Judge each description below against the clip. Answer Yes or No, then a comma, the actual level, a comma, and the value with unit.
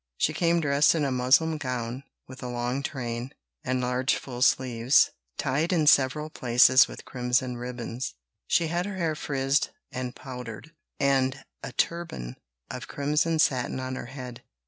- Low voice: Yes, low, 130 Hz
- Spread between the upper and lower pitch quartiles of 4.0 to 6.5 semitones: No, average, 3.3 semitones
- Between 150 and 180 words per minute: Yes, average, 155 wpm